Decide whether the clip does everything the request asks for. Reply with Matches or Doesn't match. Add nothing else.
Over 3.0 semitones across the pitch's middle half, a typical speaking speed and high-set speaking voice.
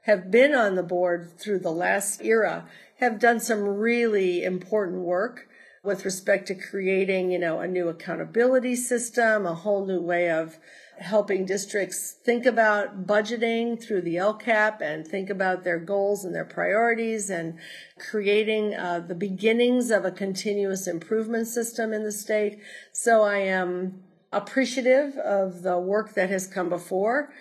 Matches